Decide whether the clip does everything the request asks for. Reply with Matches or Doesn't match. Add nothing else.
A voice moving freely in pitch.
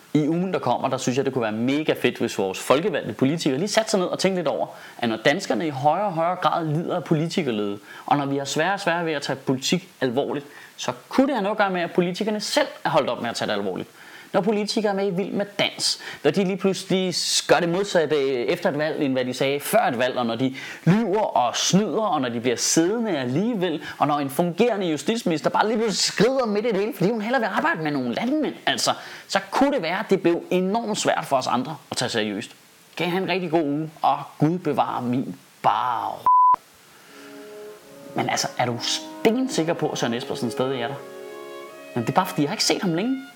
Matches